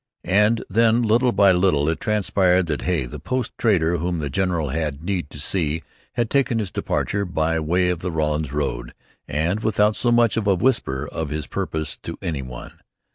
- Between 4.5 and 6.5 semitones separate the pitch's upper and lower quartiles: Yes, wide, 5.4 semitones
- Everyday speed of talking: Yes, average, 190 wpm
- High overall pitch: No, very low, 90 Hz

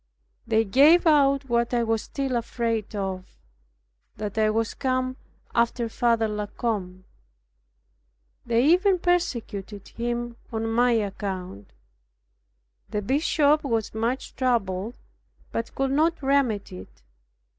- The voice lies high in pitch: Yes, high, 235 Hz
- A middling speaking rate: No, slow, 115 wpm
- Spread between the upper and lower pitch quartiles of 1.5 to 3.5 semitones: No, average, 4.1 semitones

